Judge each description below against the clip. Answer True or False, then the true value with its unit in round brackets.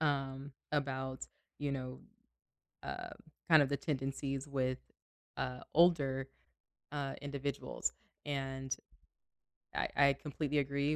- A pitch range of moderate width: False (1.4 semitones)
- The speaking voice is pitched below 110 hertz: False (140 Hz)